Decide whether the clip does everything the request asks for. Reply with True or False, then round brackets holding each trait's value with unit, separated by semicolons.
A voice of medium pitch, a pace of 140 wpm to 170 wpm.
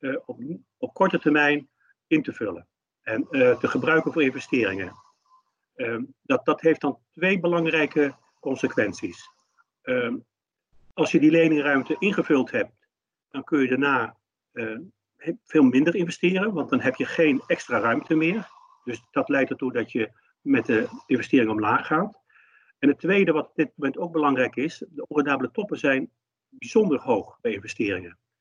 True (165 Hz; 155 wpm)